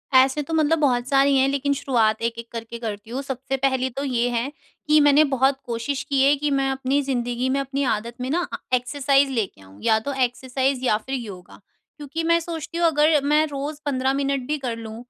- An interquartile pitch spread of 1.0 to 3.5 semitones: Yes, average, 2.8 semitones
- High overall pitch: Yes, very high, 270 Hz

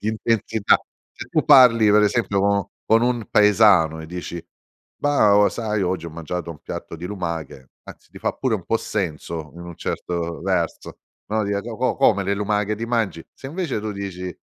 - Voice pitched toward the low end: Yes, low, 100 Hz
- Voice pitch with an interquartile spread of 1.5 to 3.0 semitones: No, average, 4.4 semitones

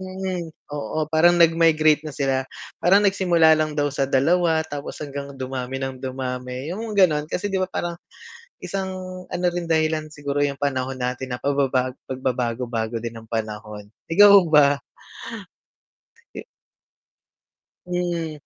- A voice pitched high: No, medium, 150 Hz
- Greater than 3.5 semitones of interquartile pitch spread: Yes, average, 4.8 semitones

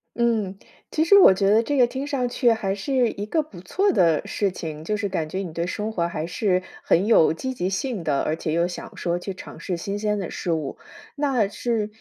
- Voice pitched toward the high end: Yes, high, 200 Hz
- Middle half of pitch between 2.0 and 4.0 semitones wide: No, wide, 5.4 semitones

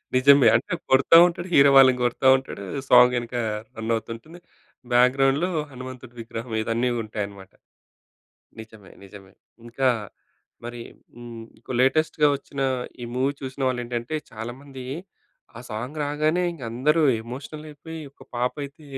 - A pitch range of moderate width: Yes, average, 3.3 semitones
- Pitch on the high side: No, low, 130 Hz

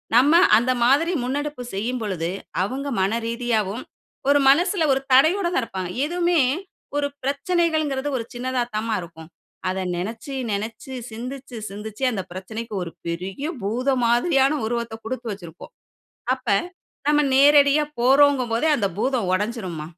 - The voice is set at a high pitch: Yes, high, 245 Hz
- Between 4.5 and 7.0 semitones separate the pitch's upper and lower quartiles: Yes, average, 4.9 semitones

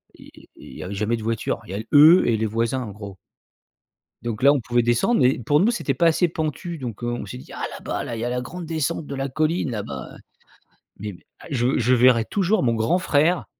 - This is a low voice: Yes, low, 125 Hz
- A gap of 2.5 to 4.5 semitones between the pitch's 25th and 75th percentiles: No, wide, 5.4 semitones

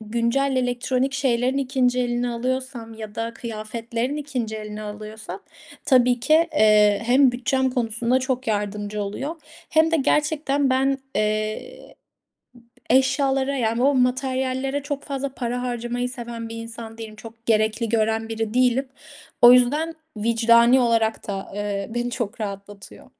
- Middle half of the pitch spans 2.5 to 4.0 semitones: Yes, average, 3.0 semitones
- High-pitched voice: Yes, high, 240 Hz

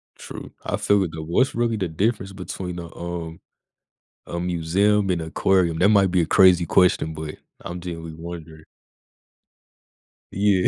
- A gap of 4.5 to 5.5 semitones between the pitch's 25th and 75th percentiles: No, average, 2.8 semitones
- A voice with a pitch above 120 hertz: No, very low, 90 Hz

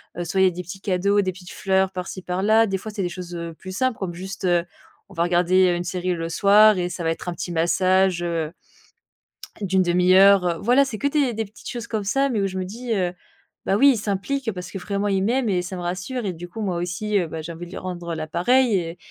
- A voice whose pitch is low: No, medium, 185 Hz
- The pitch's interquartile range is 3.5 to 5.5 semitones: No, average, 2.8 semitones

